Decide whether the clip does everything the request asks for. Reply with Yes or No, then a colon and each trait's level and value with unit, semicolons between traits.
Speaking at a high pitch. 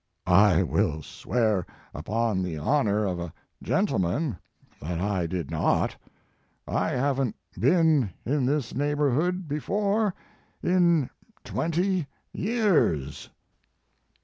No: low, 130 Hz